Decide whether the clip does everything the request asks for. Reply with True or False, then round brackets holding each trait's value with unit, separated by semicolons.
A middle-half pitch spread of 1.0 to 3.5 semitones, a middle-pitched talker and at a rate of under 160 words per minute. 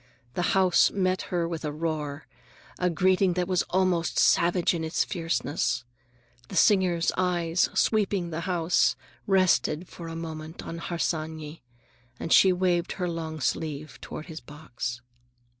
True (2.4 semitones; 170 Hz; 140 wpm)